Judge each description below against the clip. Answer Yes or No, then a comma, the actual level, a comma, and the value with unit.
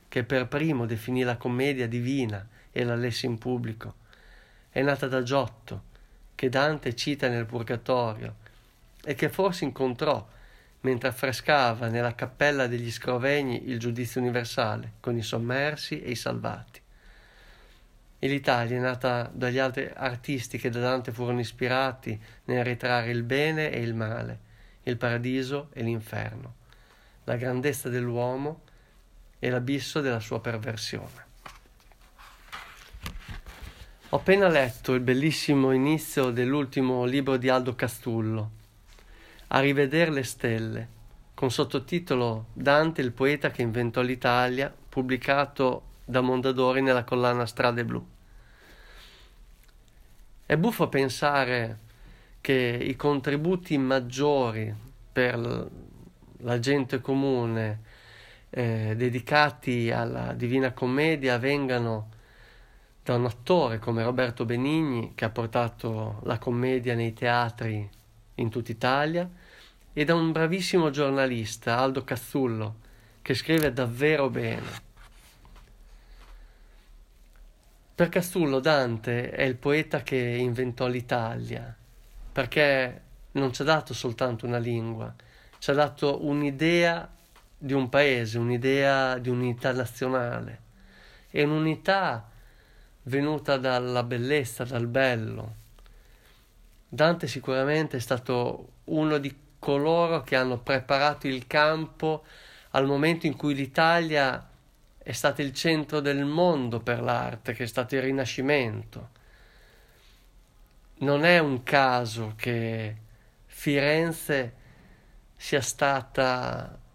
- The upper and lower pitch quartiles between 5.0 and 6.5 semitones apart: No, average, 3.0 semitones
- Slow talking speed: Yes, slow, 110 wpm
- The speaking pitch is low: Yes, low, 125 Hz